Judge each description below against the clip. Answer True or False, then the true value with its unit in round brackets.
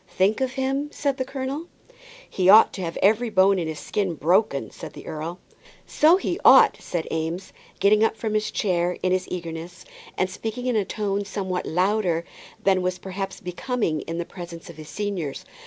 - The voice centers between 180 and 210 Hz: True (190 Hz)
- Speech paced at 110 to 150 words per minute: False (190 wpm)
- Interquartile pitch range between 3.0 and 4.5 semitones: True (4.1 semitones)